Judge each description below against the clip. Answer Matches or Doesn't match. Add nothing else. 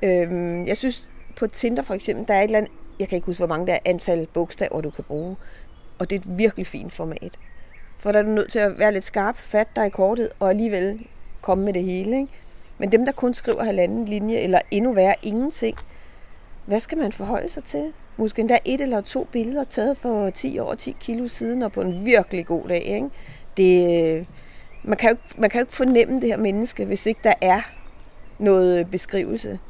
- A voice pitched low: Doesn't match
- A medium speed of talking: Matches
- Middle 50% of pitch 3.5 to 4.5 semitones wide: Matches